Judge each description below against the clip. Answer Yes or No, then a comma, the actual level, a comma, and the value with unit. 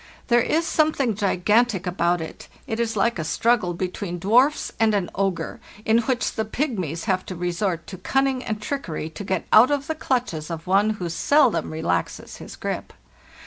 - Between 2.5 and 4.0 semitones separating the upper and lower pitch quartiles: No, wide, 5.5 semitones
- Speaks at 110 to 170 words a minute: No, average, 180 wpm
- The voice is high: Yes, high, 205 Hz